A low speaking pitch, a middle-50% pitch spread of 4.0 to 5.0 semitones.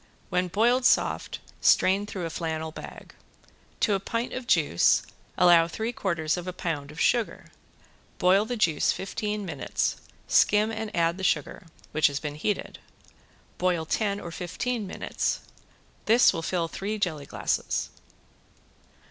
No: medium, 180 Hz; average, 4.4 semitones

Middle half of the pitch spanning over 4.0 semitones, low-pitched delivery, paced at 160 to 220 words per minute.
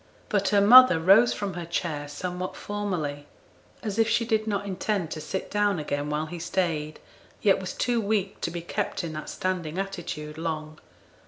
No: average, 4.6 semitones; medium, 180 Hz; average, 180 wpm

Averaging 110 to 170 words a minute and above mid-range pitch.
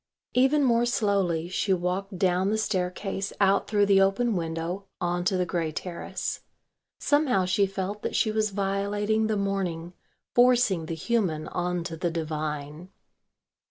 Yes: average, 150 wpm; high, 195 Hz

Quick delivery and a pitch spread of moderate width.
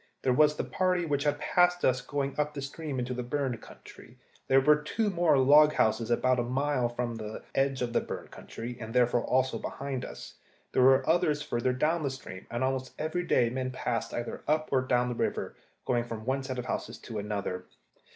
Yes: fast, 210 wpm; average, 3.4 semitones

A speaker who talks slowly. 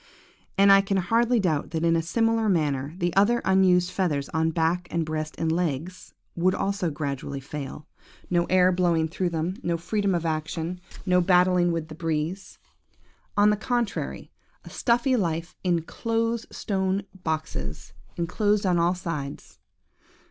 No: average, 155 wpm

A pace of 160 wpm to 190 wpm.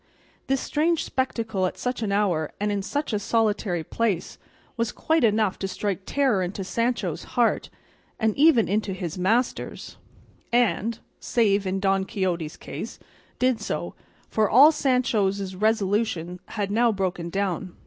No: average, 145 wpm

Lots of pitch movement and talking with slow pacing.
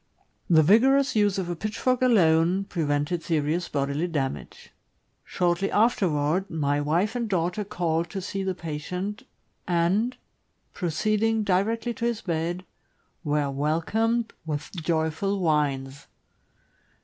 No: average, 4.8 semitones; slow, 115 wpm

